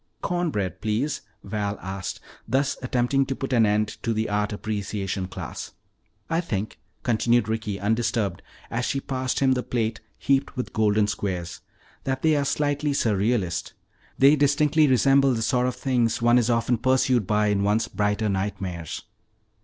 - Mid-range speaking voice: No, low, 115 Hz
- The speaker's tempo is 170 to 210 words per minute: No, average, 160 wpm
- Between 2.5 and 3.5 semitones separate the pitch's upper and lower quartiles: No, average, 4.3 semitones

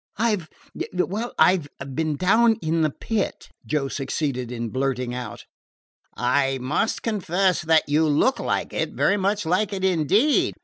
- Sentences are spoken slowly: No, average, 165 wpm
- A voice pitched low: No, medium, 160 Hz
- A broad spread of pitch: Yes, wide, 6.3 semitones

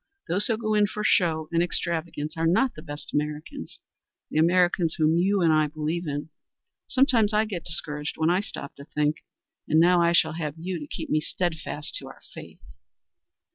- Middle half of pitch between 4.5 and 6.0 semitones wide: No, average, 2.9 semitones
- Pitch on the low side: No, medium, 165 Hz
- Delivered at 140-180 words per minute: No, average, 190 wpm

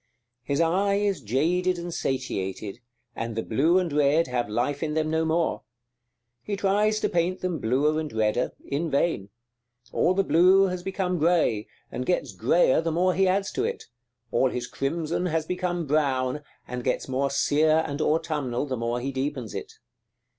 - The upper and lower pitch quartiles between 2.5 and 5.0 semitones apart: No, wide, 5.6 semitones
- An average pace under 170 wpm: No, average, 175 wpm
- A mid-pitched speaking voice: Yes, medium, 155 Hz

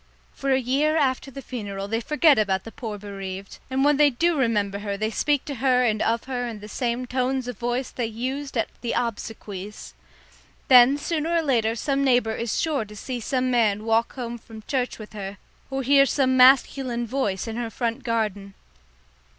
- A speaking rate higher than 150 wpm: Yes, average, 190 wpm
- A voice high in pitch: Yes, high, 240 Hz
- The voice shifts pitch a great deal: No, average, 3.7 semitones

